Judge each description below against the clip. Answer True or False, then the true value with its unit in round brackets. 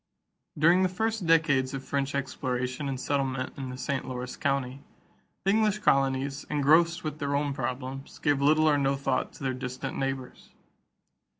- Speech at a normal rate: True (170 wpm)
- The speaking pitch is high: False (140 Hz)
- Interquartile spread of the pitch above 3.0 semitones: False (2.6 semitones)